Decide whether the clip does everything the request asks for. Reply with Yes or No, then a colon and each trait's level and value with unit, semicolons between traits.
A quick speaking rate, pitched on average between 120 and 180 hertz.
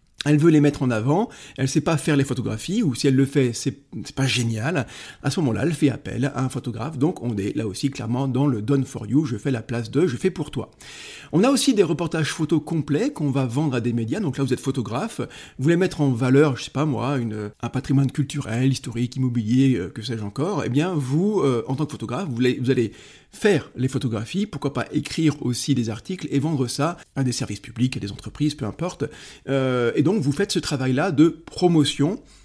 Yes: fast, 235 wpm; low, 135 Hz